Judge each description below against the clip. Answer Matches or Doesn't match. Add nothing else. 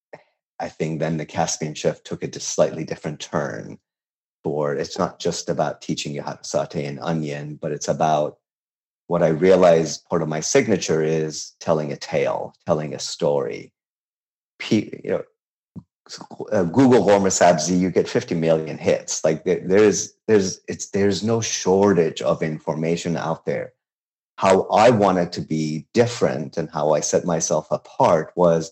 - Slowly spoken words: Doesn't match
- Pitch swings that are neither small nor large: Matches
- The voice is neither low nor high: Doesn't match